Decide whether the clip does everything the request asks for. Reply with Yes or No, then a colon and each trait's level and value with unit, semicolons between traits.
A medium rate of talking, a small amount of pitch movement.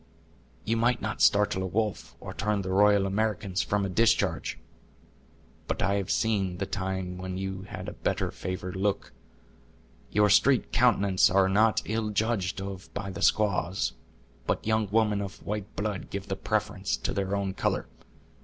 Yes: average, 165 wpm; narrow, 1.9 semitones